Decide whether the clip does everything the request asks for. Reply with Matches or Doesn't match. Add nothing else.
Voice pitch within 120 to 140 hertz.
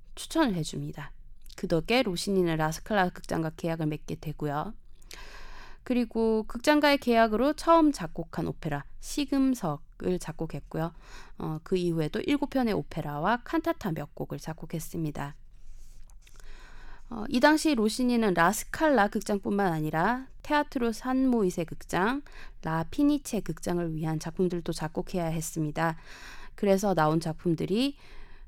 Doesn't match